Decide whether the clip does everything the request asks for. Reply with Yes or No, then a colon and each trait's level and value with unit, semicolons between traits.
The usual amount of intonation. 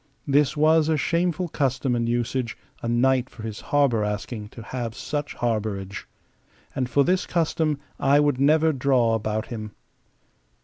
Yes: average, 4.4 semitones